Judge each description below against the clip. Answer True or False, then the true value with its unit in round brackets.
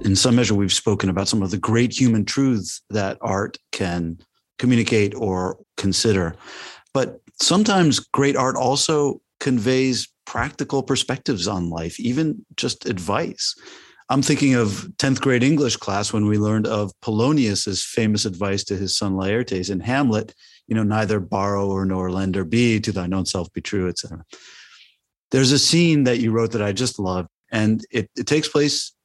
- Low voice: True (110 Hz)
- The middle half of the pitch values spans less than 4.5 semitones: False (4.9 semitones)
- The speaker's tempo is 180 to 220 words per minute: False (170 wpm)